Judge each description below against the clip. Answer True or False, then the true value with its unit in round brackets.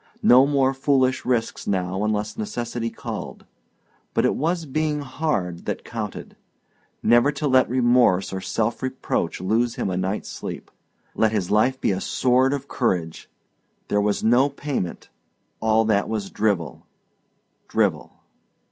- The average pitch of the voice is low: True (115 Hz)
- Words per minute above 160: False (140 wpm)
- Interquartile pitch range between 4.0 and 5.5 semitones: True (4.4 semitones)